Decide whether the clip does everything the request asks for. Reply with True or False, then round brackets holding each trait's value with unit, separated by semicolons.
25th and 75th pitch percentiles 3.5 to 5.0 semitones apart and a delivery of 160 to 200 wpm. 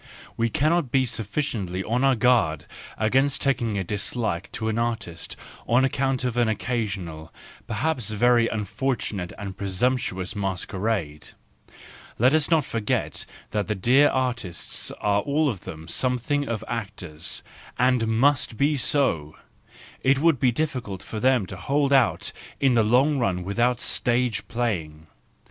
False (4.7 semitones; 140 wpm)